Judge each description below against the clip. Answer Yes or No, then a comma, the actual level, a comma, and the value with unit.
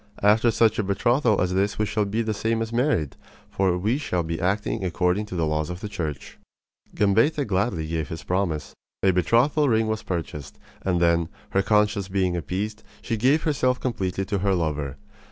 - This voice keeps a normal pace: Yes, average, 190 wpm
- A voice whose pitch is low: Yes, low, 100 Hz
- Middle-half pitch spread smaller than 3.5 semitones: No, average, 4.1 semitones